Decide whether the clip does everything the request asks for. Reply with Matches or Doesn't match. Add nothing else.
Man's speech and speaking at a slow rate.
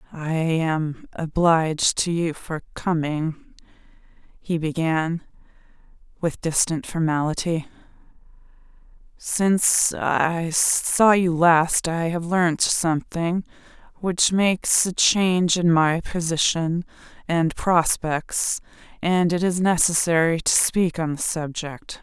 Doesn't match